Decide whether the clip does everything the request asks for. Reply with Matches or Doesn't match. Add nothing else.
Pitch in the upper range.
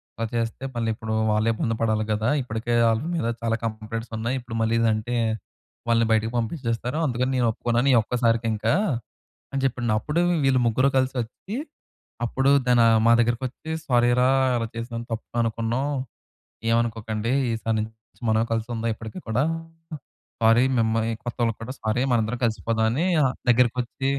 Doesn't match